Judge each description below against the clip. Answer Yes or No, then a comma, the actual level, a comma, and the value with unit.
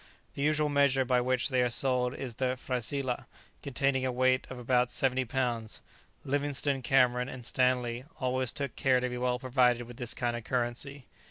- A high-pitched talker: No, low, 125 Hz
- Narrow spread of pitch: Yes, narrow, 1.5 semitones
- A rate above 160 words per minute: Yes, average, 180 wpm